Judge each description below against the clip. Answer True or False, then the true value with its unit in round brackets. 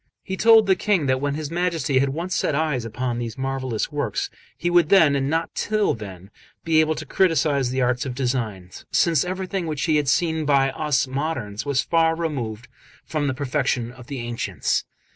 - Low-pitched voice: False (145 Hz)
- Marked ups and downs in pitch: False (4.3 semitones)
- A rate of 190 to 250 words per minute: True (195 wpm)